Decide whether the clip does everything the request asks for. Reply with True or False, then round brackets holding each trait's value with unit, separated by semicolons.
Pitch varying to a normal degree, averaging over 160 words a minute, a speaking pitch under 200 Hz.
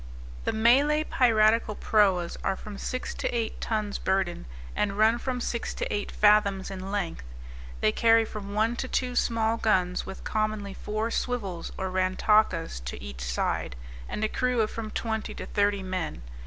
False (3.1 semitones; 170 wpm; 210 Hz)